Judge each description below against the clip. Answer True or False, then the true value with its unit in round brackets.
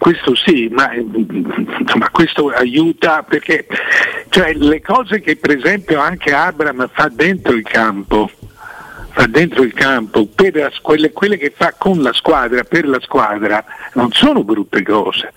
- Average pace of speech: True (150 wpm)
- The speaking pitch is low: False (155 Hz)